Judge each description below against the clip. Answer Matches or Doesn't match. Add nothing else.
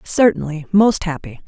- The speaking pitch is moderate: Matches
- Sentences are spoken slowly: Matches